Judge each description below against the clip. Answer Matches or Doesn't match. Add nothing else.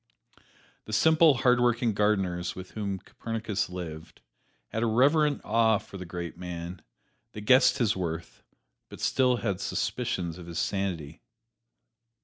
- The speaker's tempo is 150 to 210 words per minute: Doesn't match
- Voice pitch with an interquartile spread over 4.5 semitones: Matches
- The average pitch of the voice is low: Matches